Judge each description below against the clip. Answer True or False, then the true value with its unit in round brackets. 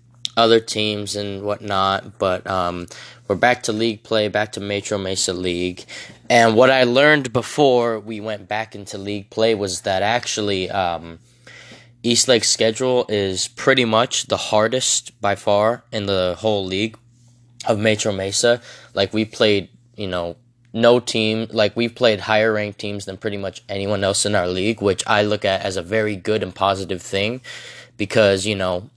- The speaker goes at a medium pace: True (170 wpm)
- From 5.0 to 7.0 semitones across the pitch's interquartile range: False (3.0 semitones)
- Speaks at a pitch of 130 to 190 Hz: False (110 Hz)